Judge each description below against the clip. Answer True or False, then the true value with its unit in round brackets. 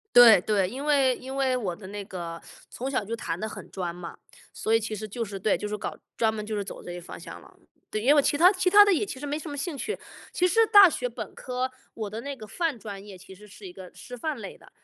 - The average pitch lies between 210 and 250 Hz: True (225 Hz)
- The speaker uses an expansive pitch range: True (5.8 semitones)